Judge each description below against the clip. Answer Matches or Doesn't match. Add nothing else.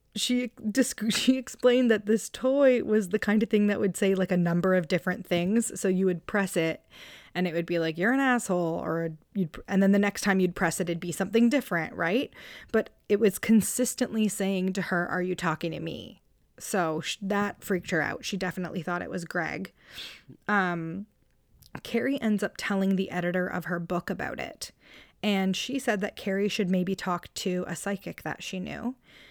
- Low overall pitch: Doesn't match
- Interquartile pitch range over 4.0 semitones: Doesn't match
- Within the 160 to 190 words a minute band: Doesn't match